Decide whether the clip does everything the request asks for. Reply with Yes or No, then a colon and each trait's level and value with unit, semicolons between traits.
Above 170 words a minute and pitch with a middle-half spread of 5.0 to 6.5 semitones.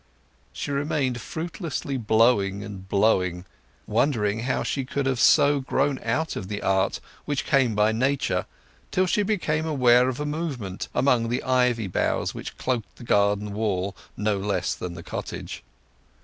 No: average, 160 wpm; average, 5.3 semitones